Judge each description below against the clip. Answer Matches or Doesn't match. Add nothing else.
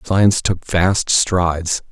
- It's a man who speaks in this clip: Matches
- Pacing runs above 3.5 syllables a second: Doesn't match